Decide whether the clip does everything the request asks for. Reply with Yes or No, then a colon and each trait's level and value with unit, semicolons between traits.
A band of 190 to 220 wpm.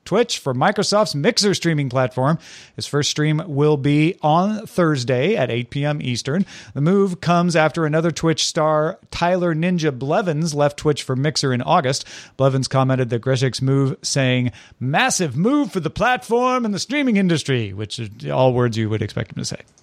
No: average, 175 wpm